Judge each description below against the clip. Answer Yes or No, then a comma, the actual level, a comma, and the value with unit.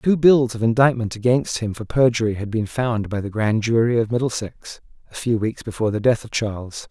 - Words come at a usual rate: No, fast, 215 wpm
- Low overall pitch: Yes, low, 115 Hz